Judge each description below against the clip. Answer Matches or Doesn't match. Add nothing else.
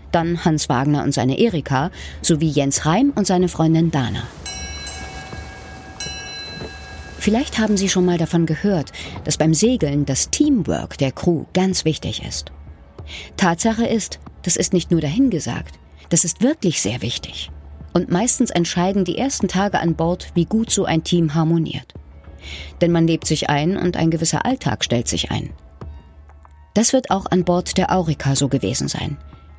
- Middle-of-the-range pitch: Matches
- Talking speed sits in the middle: Matches